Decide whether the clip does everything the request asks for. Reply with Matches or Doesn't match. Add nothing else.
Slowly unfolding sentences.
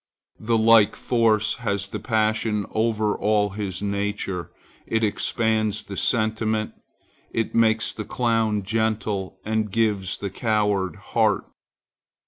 Matches